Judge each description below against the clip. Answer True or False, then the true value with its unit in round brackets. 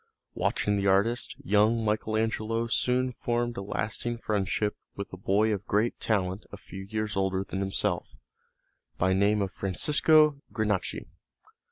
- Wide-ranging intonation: False (2.9 semitones)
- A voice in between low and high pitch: False (105 Hz)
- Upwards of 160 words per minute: False (140 wpm)